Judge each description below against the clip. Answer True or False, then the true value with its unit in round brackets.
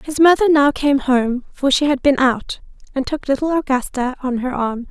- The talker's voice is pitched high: True (270 Hz)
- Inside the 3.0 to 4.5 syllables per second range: False (4.9 syllables/s)